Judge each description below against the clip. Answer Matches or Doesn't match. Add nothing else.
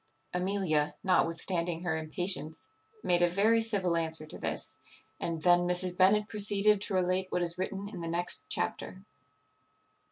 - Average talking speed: Matches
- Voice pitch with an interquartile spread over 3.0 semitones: Doesn't match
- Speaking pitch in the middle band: Matches